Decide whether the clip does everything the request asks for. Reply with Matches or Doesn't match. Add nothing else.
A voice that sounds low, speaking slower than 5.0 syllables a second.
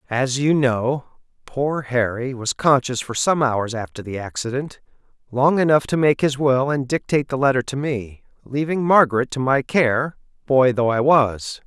Matches